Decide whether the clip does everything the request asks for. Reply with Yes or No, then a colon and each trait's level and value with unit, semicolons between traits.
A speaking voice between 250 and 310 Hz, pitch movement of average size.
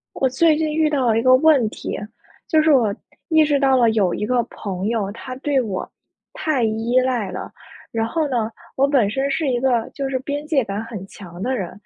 Yes: very high, 255 Hz; average, 4.3 semitones